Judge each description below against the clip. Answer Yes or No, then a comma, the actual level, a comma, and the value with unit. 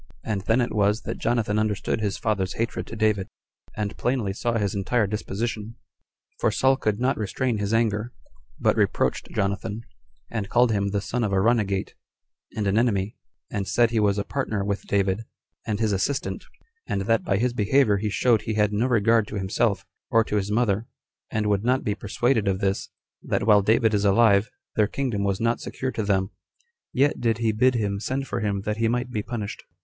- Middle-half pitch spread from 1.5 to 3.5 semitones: Yes, narrow, 2.6 semitones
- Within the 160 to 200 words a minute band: Yes, average, 195 wpm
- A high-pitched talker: No, low, 105 Hz